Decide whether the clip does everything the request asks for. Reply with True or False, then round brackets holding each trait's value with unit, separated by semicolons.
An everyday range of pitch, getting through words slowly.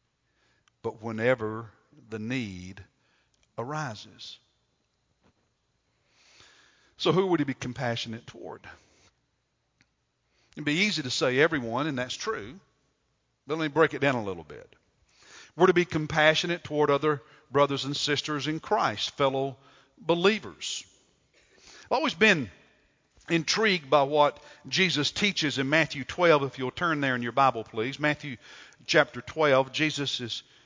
True (4.1 semitones; 130 wpm)